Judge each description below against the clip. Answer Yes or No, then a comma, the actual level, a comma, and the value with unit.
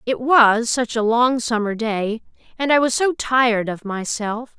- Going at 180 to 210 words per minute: Yes, average, 185 wpm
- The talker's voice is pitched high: Yes, high, 235 Hz